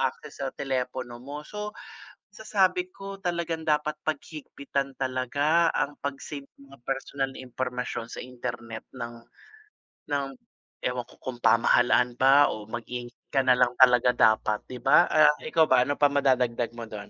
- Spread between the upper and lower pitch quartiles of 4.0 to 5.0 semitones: No, average, 3.2 semitones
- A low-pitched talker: Yes, low, 130 Hz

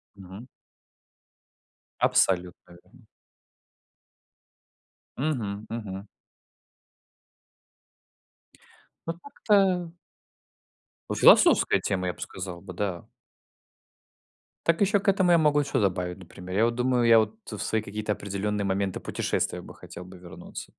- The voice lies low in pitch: Yes, low, 105 Hz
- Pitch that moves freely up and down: Yes, wide, 5.8 semitones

